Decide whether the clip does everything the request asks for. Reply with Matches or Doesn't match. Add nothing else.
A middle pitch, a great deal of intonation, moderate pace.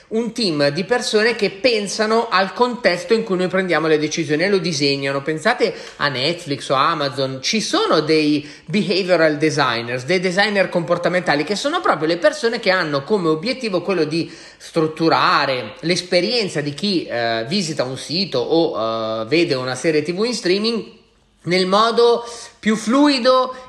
Matches